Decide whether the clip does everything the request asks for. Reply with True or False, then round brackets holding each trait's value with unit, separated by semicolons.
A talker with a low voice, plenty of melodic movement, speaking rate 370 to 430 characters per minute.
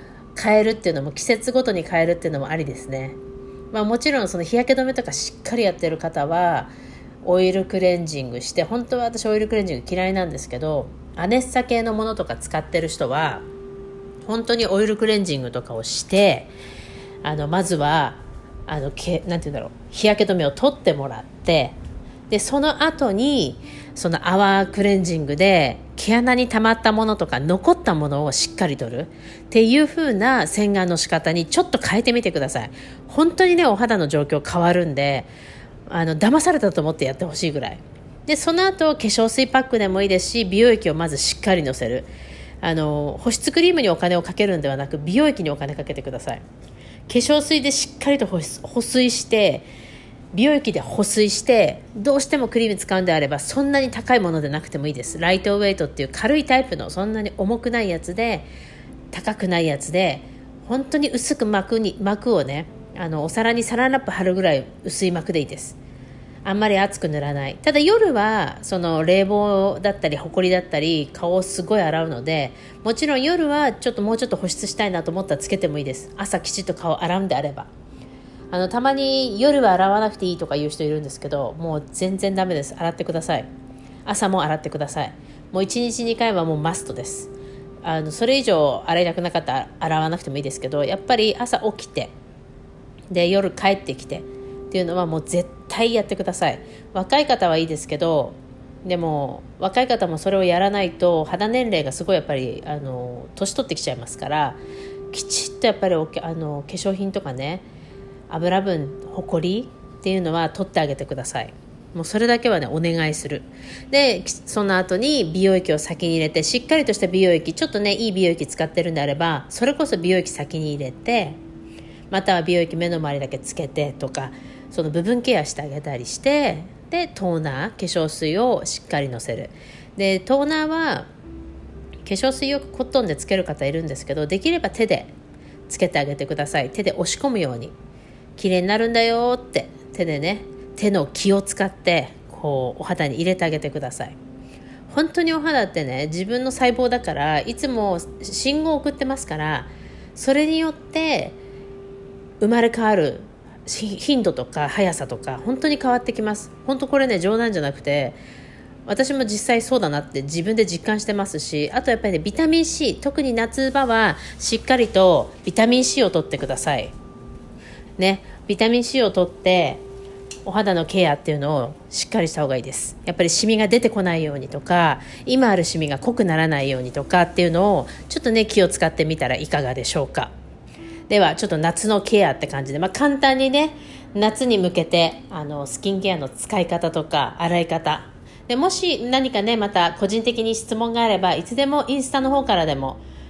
False (185 Hz; 7.1 semitones; 380 characters per minute)